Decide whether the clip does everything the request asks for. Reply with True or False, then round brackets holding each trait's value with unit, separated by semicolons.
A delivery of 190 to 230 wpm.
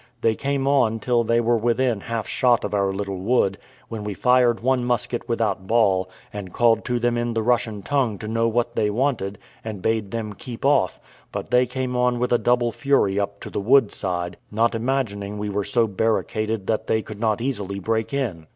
True (205 wpm)